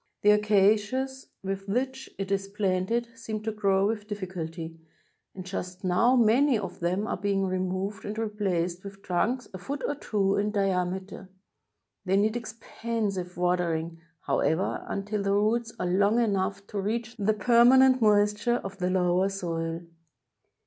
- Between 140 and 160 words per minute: Yes, average, 150 wpm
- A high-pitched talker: Yes, high, 200 Hz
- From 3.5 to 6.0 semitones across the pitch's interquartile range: No, average, 3.0 semitones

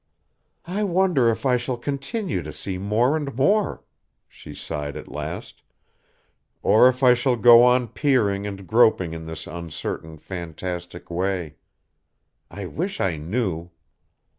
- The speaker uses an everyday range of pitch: No, wide, 7.0 semitones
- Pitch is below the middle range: Yes, low, 110 Hz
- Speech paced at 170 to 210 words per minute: No, average, 140 wpm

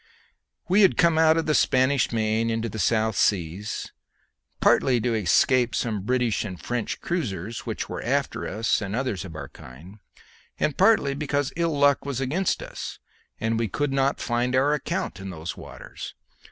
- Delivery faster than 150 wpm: Yes, average, 170 wpm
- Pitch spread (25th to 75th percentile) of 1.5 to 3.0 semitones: No, average, 5.2 semitones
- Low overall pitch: Yes, low, 120 Hz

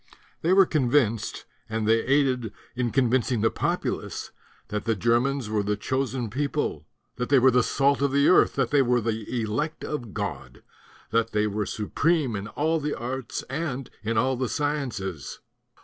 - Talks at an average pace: Yes, average, 170 wpm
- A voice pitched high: No, low, 125 Hz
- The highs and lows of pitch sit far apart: No, average, 3.9 semitones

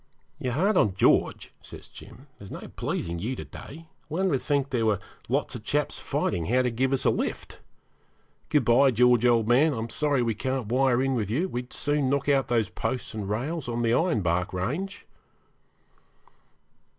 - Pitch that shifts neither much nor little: Yes, average, 3.8 semitones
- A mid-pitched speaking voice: No, low, 125 Hz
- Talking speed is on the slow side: No, average, 185 wpm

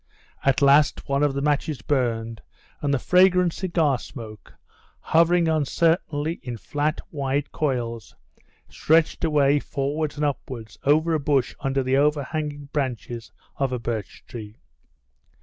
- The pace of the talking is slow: Yes, slow, 130 wpm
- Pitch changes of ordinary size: Yes, average, 3.3 semitones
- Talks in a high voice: No, medium, 145 Hz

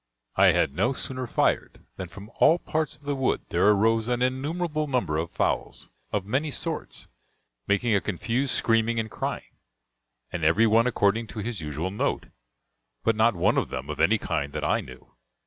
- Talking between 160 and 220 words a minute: Yes, average, 180 wpm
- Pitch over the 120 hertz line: No, low, 115 Hz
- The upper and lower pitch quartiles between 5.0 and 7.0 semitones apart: No, average, 4.6 semitones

